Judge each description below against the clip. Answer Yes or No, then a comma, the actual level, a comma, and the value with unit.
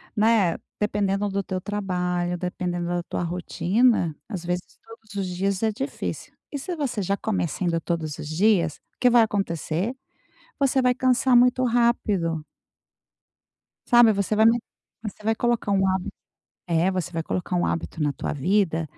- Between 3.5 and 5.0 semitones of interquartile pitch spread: Yes, average, 4.4 semitones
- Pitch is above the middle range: Yes, high, 195 Hz